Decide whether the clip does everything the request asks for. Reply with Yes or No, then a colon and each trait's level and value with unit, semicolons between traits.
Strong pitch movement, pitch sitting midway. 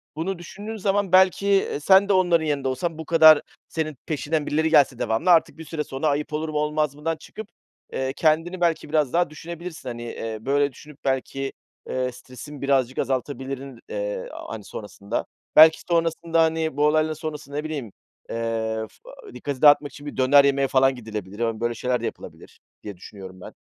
No: average, 3.8 semitones; medium, 150 Hz